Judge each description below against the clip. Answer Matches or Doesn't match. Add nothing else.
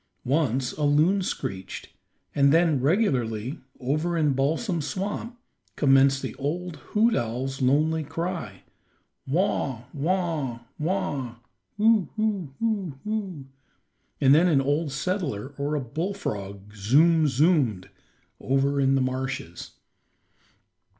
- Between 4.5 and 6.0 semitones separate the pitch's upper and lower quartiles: Matches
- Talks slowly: Matches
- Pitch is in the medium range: Matches